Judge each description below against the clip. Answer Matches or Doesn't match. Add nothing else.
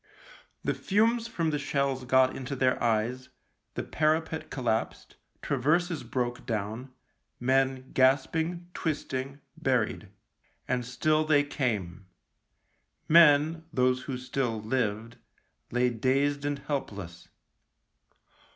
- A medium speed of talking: Doesn't match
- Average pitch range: Matches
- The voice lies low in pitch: Matches